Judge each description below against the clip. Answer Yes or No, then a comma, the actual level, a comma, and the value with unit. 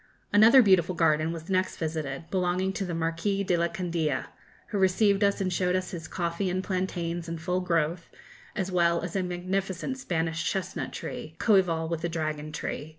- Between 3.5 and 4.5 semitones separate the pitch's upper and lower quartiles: No, narrow, 2.4 semitones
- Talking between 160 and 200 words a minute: Yes, average, 180 wpm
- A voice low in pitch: No, medium, 175 Hz